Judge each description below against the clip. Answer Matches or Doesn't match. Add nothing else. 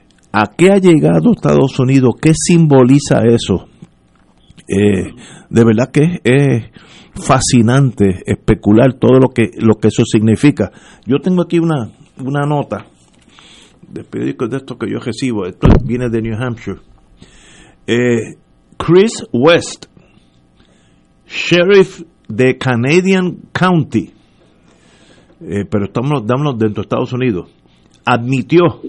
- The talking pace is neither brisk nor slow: Doesn't match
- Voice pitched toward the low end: Matches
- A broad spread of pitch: Matches